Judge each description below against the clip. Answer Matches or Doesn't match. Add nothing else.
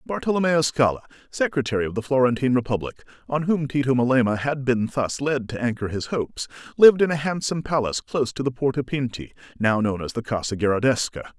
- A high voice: Doesn't match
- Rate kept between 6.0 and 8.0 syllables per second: Matches